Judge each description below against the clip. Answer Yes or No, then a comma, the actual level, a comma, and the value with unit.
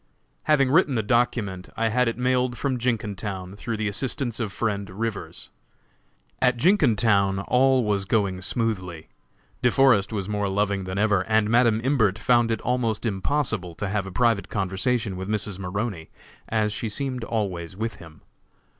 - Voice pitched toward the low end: Yes, low, 110 Hz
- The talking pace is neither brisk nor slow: Yes, average, 160 wpm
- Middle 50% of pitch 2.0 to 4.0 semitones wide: Yes, average, 3.7 semitones